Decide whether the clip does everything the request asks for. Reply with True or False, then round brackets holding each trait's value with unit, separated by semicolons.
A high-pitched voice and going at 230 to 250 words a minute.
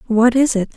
True (235 Hz; 235 wpm)